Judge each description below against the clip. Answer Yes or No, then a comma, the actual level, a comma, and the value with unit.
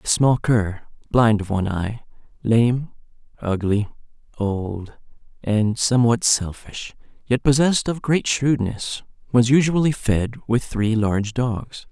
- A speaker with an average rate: No, slow, 125 wpm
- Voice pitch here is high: No, low, 115 Hz